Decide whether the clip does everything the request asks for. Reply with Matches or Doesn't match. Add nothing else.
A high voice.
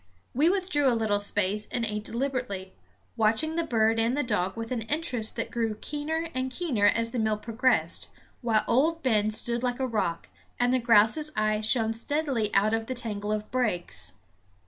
Matches